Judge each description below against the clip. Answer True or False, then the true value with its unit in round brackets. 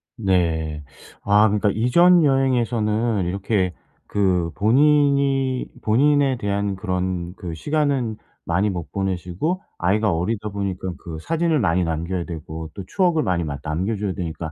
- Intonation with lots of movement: True (6.3 semitones)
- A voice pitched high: False (100 Hz)